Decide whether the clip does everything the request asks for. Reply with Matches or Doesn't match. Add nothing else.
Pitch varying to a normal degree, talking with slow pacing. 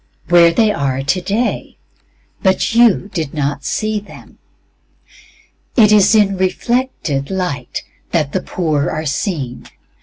Doesn't match